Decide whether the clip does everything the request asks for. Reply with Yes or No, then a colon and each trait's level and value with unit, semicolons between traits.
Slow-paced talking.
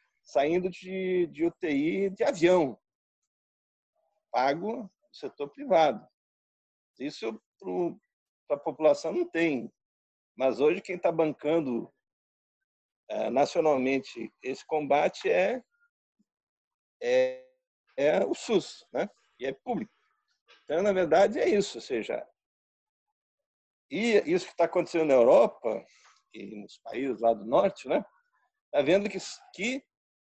Yes: slow, 115 wpm